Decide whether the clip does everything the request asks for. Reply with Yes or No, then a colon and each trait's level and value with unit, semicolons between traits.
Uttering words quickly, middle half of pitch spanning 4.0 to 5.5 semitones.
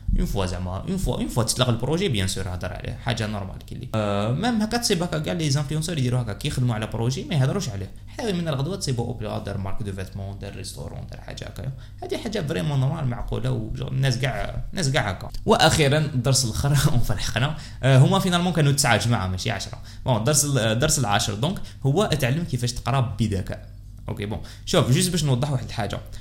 Yes: fast, 200 wpm; average, 5.0 semitones